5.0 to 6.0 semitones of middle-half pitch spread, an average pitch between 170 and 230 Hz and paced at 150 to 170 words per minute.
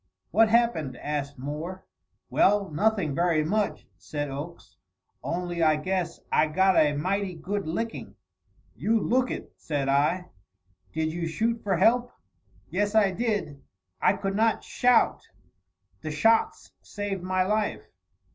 No: average, 5.3 semitones; medium, 185 Hz; slow, 135 wpm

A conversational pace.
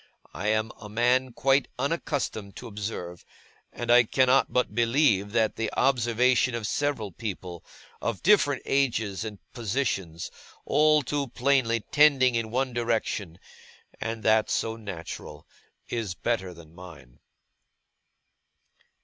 No: slow, 125 wpm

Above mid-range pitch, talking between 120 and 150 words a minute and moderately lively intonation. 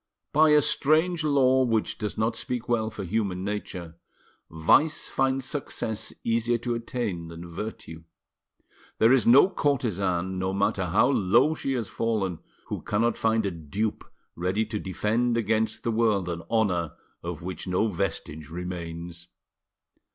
No: low, 110 Hz; average, 145 wpm; average, 4.8 semitones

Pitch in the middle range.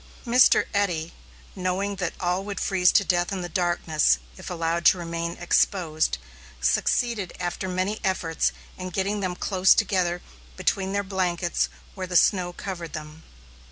Yes: medium, 180 Hz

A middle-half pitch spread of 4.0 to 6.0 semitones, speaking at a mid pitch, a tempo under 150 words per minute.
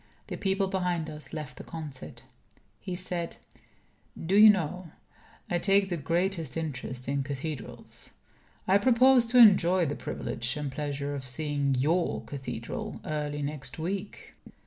Yes: average, 5.0 semitones; medium, 160 Hz; average, 140 wpm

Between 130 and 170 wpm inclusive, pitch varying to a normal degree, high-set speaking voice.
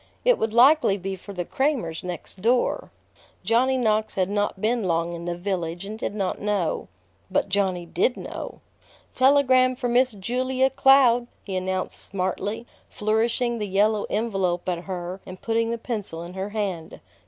Yes: average, 165 wpm; average, 4.4 semitones; high, 205 Hz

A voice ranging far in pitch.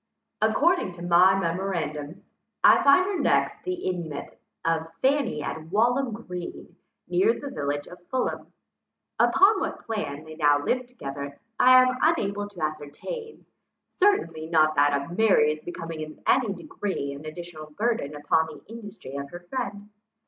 Yes: wide, 7.8 semitones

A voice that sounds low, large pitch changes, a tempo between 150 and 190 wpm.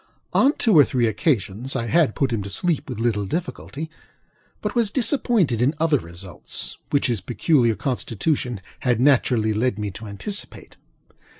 Yes: low, 125 Hz; wide, 6.6 semitones; average, 160 wpm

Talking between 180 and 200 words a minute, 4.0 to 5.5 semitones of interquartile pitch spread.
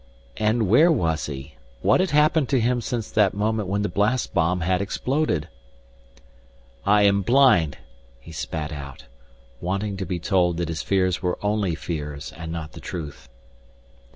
No: average, 160 wpm; average, 5.0 semitones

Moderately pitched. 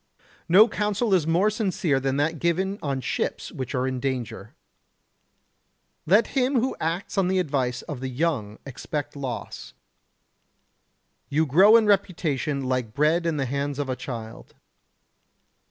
Yes: medium, 150 Hz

